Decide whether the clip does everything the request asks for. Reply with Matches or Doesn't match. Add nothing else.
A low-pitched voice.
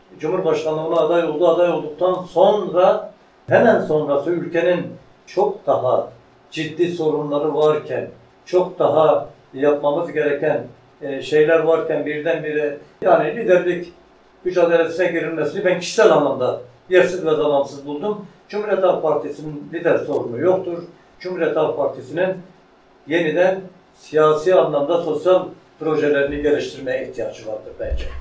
Doesn't match